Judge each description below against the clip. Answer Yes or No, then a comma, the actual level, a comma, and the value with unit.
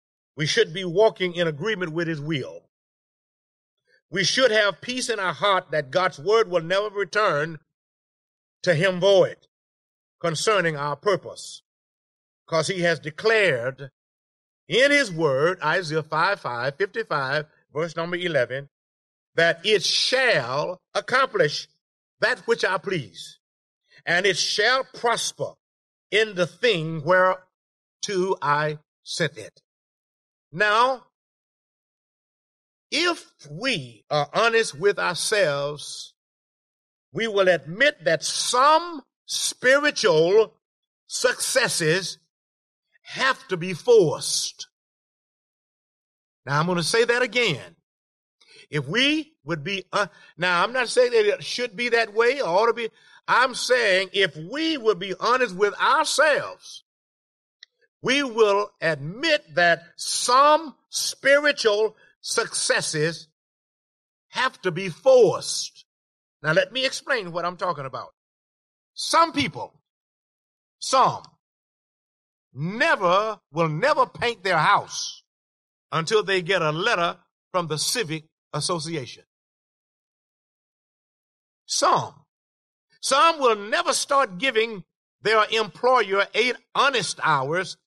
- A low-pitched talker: No, high, 195 Hz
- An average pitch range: No, wide, 7.8 semitones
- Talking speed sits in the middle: No, slow, 110 wpm